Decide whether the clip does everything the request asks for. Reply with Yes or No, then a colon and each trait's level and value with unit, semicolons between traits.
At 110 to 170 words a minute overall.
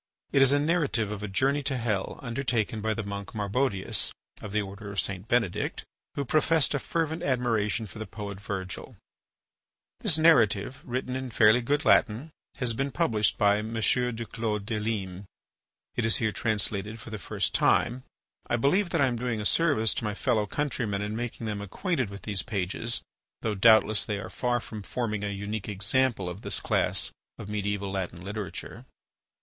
No: average, 180 wpm